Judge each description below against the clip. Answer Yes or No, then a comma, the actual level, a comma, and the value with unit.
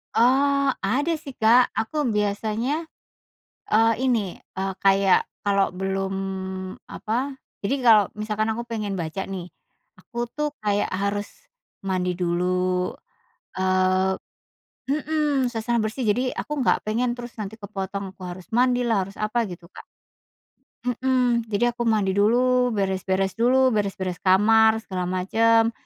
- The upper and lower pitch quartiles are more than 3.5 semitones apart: Yes, average, 4.1 semitones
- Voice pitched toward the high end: Yes, high, 215 Hz